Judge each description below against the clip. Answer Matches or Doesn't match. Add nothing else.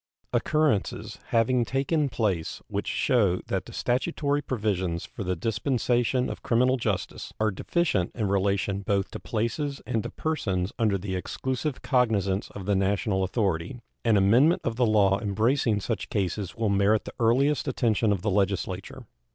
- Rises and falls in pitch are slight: Doesn't match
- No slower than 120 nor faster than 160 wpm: Matches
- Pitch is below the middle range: Matches